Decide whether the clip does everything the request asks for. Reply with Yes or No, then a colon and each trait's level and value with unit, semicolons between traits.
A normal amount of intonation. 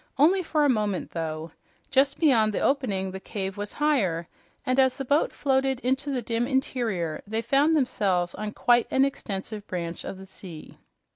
No: wide, 6.1 semitones